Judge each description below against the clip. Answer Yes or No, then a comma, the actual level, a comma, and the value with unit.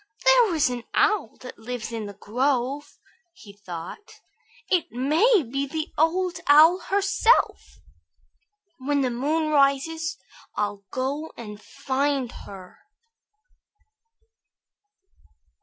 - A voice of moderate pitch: No, very high, 280 Hz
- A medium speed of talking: No, slow, 105 wpm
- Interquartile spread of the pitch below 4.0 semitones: No, wide, 5.4 semitones